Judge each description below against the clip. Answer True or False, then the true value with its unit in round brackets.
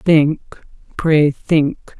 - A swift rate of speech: False (90 wpm)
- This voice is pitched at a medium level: True (155 Hz)